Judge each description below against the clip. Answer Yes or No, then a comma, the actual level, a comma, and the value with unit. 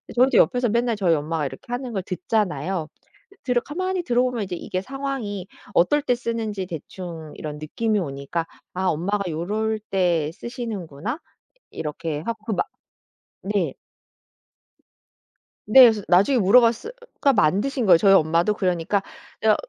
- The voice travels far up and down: Yes, wide, 5.9 semitones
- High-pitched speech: Yes, high, 200 Hz